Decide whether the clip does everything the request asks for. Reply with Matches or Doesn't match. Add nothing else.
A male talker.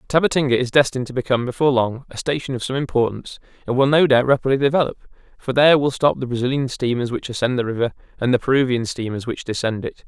Matches